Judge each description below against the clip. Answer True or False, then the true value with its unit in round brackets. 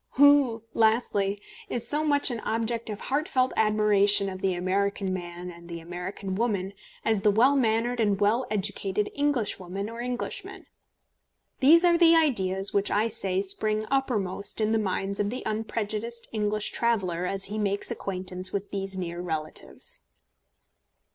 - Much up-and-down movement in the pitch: False (3.3 semitones)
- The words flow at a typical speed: True (155 wpm)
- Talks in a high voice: True (210 Hz)